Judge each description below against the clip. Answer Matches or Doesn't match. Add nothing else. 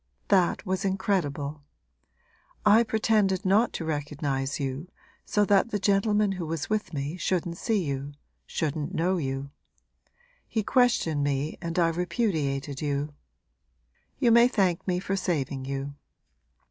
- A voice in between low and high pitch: Matches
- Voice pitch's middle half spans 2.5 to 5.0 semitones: Doesn't match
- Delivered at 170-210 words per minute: Doesn't match